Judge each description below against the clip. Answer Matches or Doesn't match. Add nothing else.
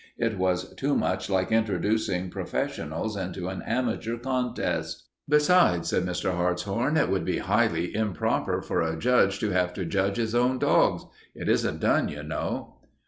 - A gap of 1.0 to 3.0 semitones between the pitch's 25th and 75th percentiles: Doesn't match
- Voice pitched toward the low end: Matches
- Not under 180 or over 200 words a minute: Doesn't match